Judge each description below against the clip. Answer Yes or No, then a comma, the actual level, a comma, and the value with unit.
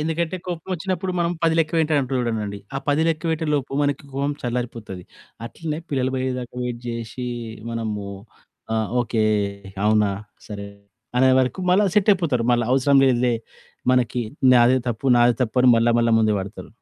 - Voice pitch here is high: No, low, 125 Hz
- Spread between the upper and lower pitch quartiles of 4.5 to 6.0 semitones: Yes, average, 4.8 semitones